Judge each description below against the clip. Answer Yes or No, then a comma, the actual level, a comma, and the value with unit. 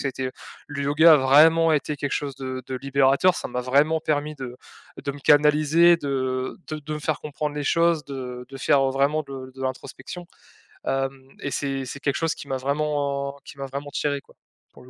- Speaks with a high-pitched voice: No, medium, 140 Hz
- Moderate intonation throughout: No, narrow, 2.1 semitones